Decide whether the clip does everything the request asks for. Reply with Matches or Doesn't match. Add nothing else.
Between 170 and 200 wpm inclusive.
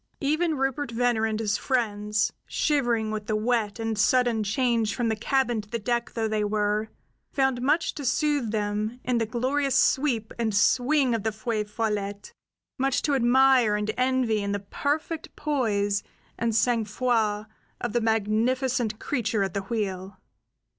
Doesn't match